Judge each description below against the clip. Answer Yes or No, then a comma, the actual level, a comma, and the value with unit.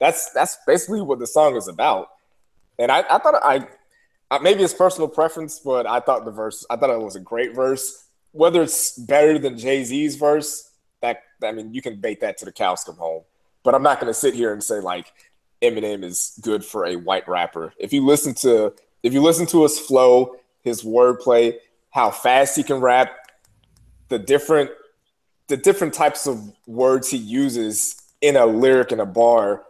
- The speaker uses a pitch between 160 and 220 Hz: No, low, 135 Hz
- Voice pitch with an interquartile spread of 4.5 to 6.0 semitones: Yes, wide, 5.5 semitones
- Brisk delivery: No, average, 195 wpm